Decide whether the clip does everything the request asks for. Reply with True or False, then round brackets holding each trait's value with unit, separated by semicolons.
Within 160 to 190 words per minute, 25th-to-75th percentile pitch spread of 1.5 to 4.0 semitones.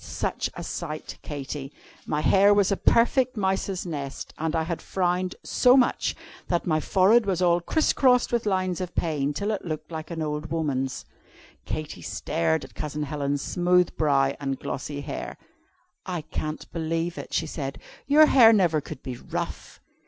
False (170 wpm; 4.4 semitones)